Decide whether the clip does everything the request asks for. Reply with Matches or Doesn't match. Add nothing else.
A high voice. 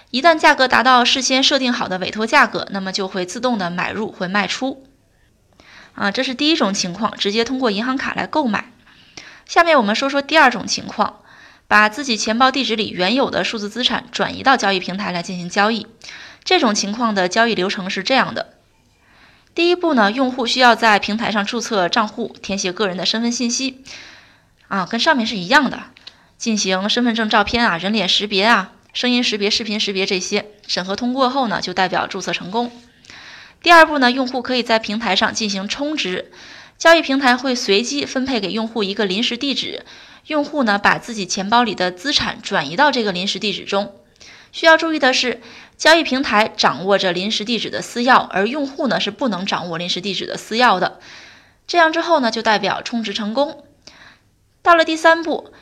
Matches